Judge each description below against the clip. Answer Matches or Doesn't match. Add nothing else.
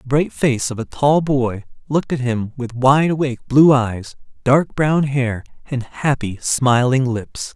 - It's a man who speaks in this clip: Matches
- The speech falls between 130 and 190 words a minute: Matches